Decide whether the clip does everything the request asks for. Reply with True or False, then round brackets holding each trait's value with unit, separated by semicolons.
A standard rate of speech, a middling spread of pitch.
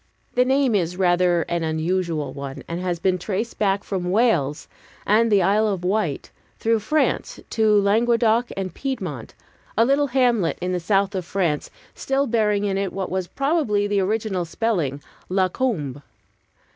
True (160 wpm; 4.3 semitones)